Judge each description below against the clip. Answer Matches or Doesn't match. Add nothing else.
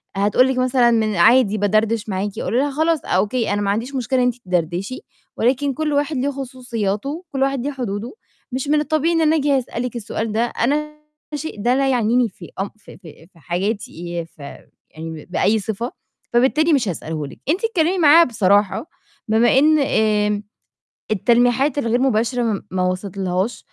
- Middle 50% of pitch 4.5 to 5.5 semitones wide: Matches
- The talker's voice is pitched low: Doesn't match